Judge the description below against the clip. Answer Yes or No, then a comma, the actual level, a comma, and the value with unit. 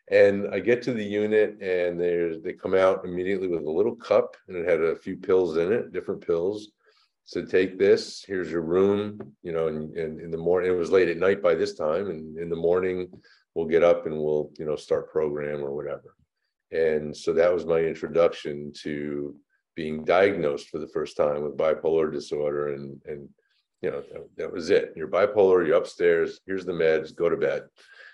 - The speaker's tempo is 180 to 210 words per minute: Yes, fast, 205 wpm